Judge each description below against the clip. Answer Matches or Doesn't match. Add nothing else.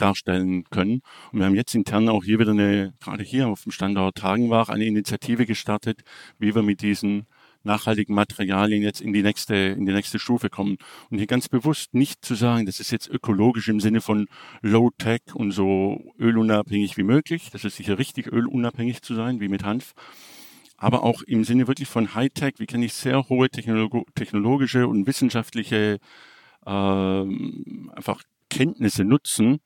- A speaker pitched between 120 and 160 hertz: Doesn't match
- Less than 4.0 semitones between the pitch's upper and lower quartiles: Matches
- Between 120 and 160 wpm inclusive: Doesn't match